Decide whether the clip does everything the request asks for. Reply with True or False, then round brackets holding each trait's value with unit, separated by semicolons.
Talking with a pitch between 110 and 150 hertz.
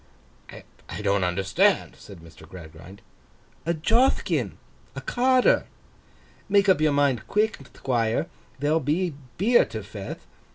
True (140 Hz)